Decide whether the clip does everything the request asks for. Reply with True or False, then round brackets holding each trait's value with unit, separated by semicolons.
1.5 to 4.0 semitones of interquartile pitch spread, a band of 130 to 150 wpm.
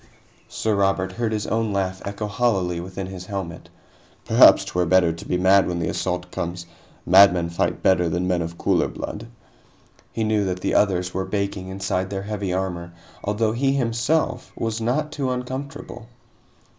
False (3.6 semitones; 170 wpm)